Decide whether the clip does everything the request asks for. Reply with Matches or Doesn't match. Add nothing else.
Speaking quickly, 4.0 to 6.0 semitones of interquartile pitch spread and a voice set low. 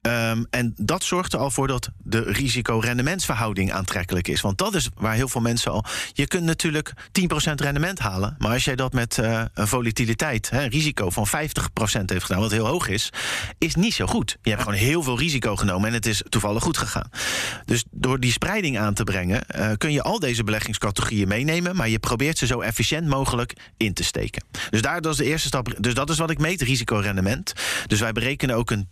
Matches